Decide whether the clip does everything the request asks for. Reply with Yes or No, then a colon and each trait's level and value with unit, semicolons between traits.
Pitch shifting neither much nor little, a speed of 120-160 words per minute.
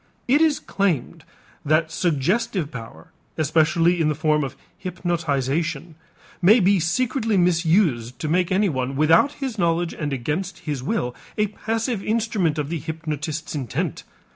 Yes: average, 4.5 semitones; average, 140 wpm